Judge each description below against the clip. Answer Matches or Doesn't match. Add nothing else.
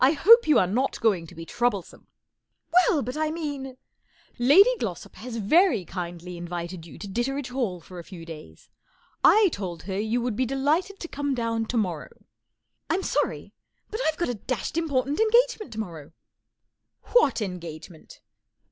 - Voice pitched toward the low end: Doesn't match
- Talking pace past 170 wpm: Matches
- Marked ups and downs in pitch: Matches